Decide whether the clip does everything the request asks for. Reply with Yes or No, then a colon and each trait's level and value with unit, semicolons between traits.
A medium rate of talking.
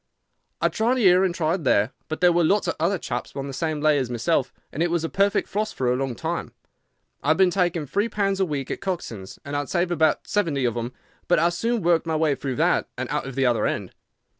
No: fast, 255 wpm